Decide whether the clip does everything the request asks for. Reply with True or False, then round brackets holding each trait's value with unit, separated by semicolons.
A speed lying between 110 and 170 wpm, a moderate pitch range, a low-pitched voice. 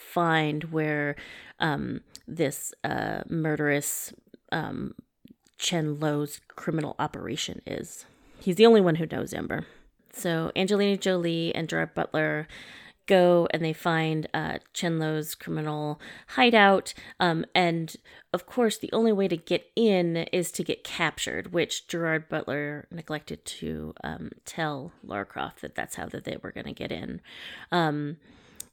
False (140 wpm; 3.0 semitones; 165 Hz)